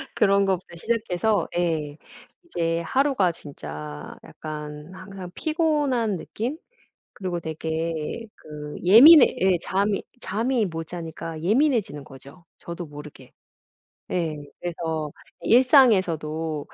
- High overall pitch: No, medium, 175 Hz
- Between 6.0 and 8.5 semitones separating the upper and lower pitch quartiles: No, wide, 5.6 semitones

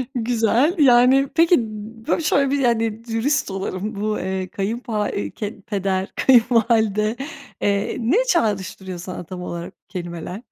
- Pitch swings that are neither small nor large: Yes, average, 4.2 semitones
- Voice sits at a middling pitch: No, high, 215 Hz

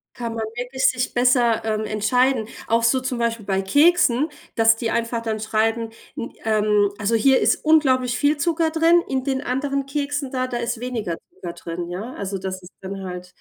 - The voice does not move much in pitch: No, average, 3.6 semitones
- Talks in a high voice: Yes, high, 235 Hz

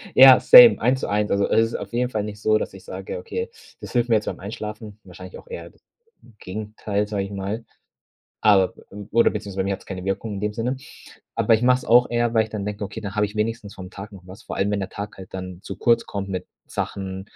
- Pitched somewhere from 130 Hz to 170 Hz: No, low, 105 Hz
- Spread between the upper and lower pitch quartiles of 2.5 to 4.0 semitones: Yes, average, 2.8 semitones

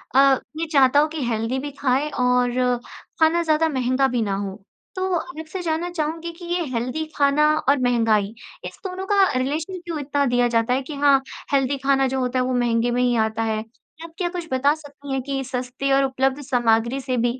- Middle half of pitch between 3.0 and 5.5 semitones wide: Yes, average, 3.7 semitones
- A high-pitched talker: Yes, very high, 270 Hz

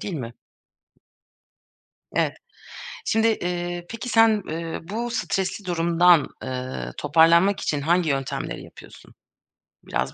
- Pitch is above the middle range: No, medium, 175 Hz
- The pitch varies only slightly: No, average, 3.9 semitones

